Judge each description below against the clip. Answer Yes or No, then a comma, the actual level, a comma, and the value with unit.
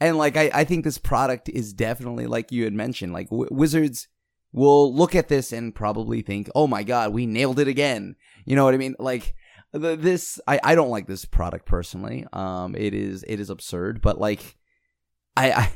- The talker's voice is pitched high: No, low, 120 Hz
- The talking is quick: Yes, fast, 210 wpm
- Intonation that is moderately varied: No, wide, 5.9 semitones